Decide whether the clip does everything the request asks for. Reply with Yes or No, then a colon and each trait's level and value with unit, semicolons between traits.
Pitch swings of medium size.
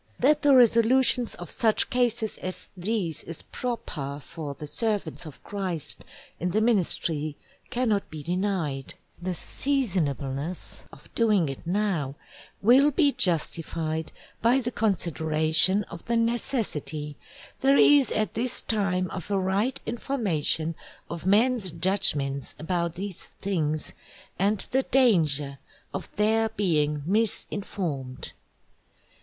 No: wide, 6.4 semitones